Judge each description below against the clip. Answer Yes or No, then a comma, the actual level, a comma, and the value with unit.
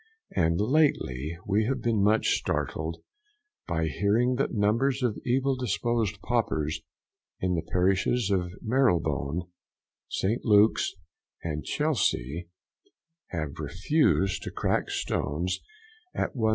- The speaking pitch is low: Yes, low, 100 Hz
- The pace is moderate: No, slow, 110 wpm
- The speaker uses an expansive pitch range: Yes, wide, 6.3 semitones